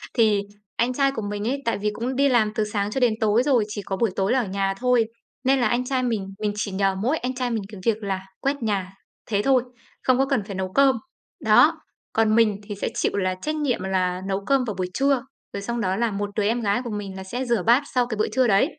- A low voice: No, high, 220 Hz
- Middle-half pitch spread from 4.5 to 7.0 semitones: No, average, 4.0 semitones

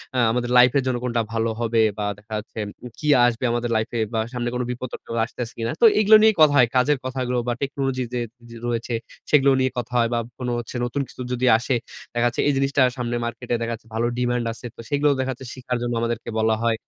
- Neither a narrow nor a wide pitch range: No, narrow, 1.7 semitones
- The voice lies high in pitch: No, low, 120 Hz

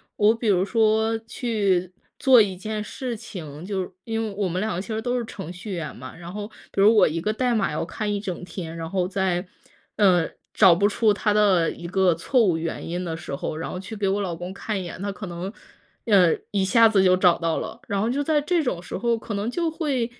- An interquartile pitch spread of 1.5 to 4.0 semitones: Yes, average, 3.7 semitones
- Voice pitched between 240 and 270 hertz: No, high, 200 Hz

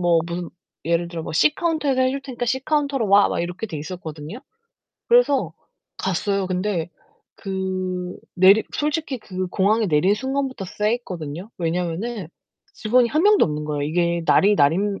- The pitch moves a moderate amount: No, wide, 6.2 semitones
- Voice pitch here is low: No, high, 190 Hz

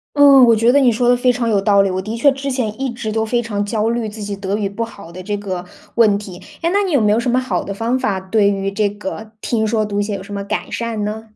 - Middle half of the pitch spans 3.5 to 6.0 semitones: No, average, 2.9 semitones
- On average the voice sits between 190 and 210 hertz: No, high, 220 Hz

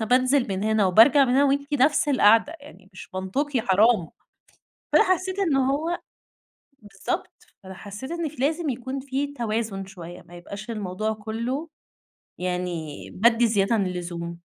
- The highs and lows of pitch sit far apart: Yes, wide, 6.4 semitones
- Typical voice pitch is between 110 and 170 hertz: No, high, 230 Hz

